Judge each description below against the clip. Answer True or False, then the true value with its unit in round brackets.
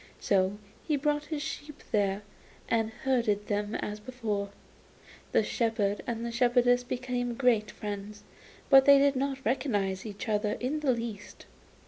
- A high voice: True (235 Hz)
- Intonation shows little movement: False (4.0 semitones)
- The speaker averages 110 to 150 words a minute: True (140 wpm)